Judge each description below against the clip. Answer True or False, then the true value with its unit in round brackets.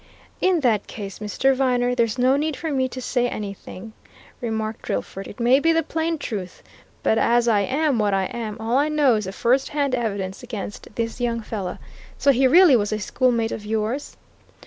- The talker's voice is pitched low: False (235 Hz)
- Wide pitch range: False (4.0 semitones)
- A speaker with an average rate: True (195 wpm)